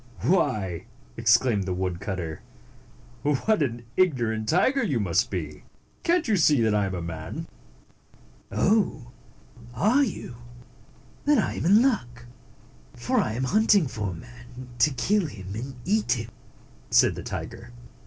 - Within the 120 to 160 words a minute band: Yes, average, 145 wpm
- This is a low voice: Yes, low, 120 Hz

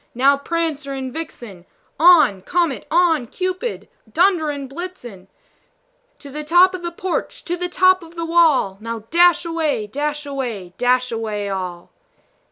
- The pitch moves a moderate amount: No, wide, 6.3 semitones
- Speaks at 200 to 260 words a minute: No, average, 155 wpm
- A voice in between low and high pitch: No, very high, 295 Hz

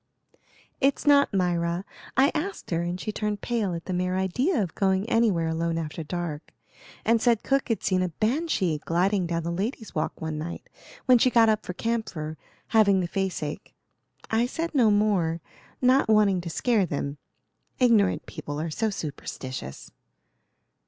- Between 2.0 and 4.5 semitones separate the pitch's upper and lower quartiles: No, average, 5.3 semitones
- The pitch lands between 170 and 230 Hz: Yes, high, 190 Hz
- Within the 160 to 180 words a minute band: Yes, average, 165 wpm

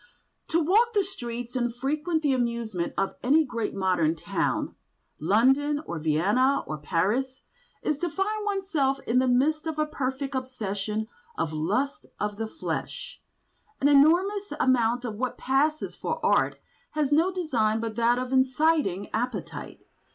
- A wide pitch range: Yes, wide, 5.8 semitones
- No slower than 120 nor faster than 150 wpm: Yes, average, 145 wpm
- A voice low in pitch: No, very high, 255 Hz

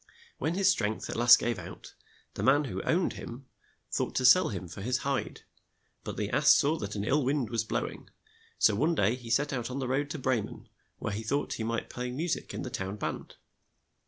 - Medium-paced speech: No, fast, 230 wpm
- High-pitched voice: No, low, 125 Hz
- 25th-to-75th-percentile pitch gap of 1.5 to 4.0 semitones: No, average, 4.4 semitones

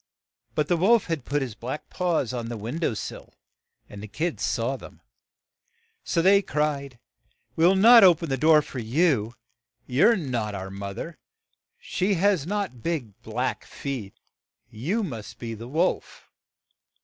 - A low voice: No, medium, 145 Hz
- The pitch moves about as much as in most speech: No, wide, 7.0 semitones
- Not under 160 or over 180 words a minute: Yes, average, 165 wpm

